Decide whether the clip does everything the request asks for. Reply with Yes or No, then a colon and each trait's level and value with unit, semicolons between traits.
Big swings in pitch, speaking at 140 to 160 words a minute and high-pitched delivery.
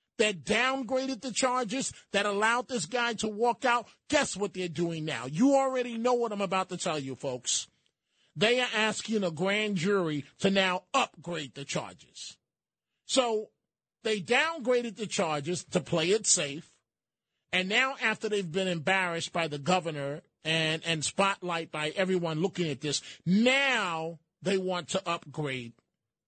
Yes: wide, 6.1 semitones; average, 155 wpm; high, 195 Hz